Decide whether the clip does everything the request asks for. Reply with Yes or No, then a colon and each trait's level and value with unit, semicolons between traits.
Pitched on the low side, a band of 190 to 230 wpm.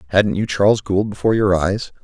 Yes: low, 100 Hz; fast, 205 wpm